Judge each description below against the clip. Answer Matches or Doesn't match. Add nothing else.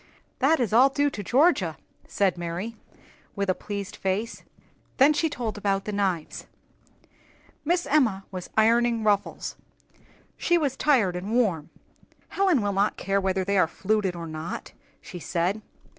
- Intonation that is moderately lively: Matches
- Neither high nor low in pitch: Doesn't match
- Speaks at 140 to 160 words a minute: Matches